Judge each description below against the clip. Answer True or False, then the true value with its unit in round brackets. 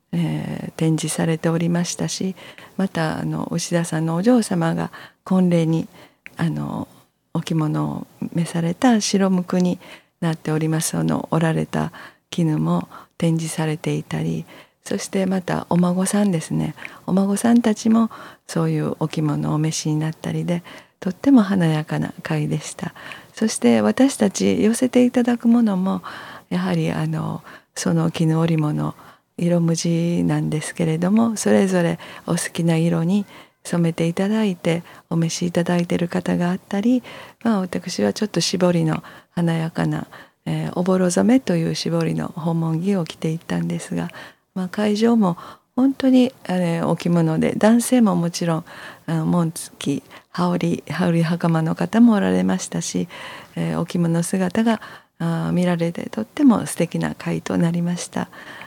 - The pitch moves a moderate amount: True (3.4 semitones)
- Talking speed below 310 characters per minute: True (300 characters per minute)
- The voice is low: False (170 Hz)